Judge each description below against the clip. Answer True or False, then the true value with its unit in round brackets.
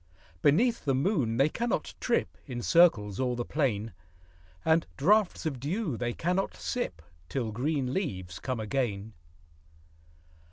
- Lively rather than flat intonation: True (6.8 semitones)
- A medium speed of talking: False (130 wpm)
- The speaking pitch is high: False (135 Hz)